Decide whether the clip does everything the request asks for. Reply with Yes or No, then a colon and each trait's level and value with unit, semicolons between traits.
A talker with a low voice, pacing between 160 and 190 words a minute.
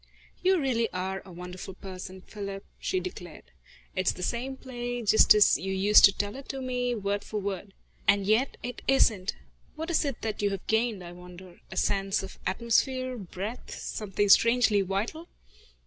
No: high, 205 Hz; average, 170 wpm